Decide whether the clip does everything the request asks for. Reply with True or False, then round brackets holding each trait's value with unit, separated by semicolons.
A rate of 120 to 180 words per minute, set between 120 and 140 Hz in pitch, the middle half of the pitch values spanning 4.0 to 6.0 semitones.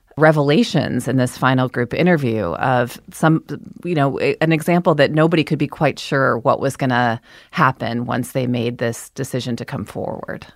True (175 wpm; 135 Hz; 4.4 semitones)